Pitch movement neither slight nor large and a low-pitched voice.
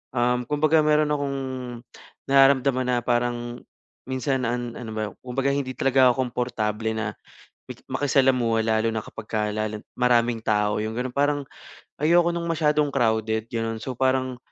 Yes: average, 3.3 semitones; low, 125 Hz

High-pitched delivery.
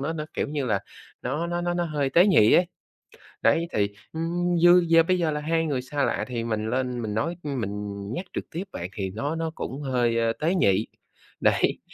No: medium, 145 Hz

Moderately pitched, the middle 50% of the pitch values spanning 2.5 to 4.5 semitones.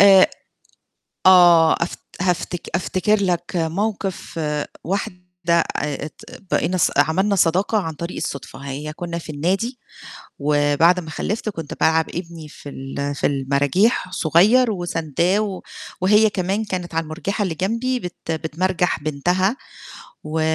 Yes: medium, 175 Hz; average, 3.4 semitones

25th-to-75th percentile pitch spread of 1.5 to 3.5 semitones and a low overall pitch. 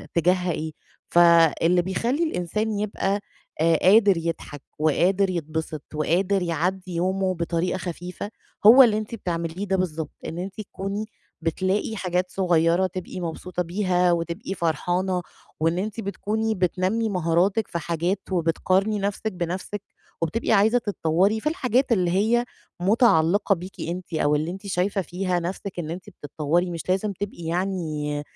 No: average, 2.9 semitones; medium, 185 Hz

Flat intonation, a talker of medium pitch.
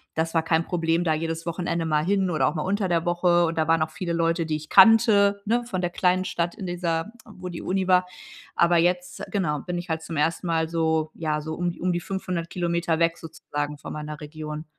Yes: narrow, 2.1 semitones; medium, 170 Hz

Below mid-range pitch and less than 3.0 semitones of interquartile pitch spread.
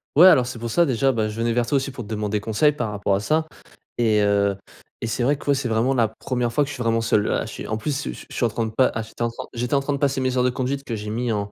No: low, 120 Hz; average, 3.6 semitones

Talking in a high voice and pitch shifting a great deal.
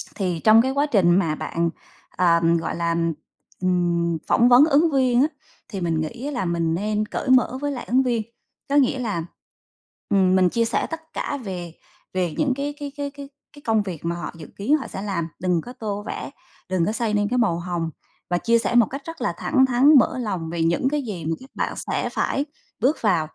Yes: high, 210 Hz; wide, 7.1 semitones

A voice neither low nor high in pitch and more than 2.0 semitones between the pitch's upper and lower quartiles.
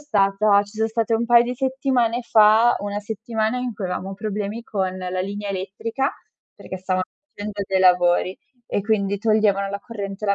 No: high, 205 Hz; narrow, 2.6 semitones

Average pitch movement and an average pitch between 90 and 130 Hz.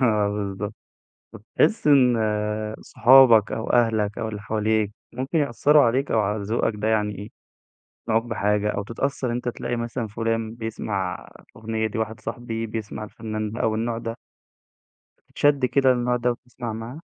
No: narrow, 2.3 semitones; low, 115 Hz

